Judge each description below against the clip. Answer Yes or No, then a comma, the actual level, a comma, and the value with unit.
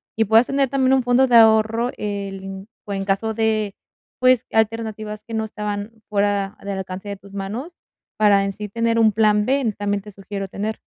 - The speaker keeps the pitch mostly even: Yes, narrow, 2.1 semitones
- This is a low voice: No, high, 215 Hz